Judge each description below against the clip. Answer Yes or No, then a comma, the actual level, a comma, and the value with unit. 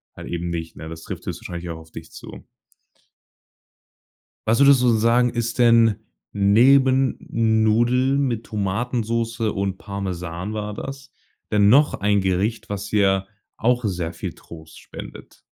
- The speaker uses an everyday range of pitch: Yes, average, 4.0 semitones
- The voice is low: Yes, low, 105 Hz